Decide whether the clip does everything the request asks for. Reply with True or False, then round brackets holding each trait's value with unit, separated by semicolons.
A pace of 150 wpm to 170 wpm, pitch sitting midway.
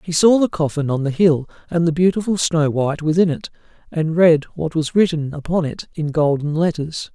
False (200 wpm; 160 Hz)